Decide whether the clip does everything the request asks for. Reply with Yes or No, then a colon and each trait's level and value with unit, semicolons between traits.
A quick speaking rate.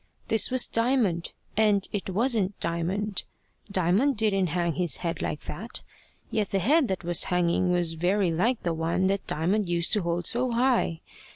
No: average, 170 wpm